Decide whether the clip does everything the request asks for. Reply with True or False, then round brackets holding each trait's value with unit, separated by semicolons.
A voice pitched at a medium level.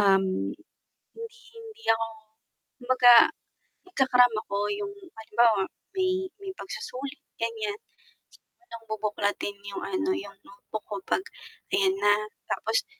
False (250 Hz)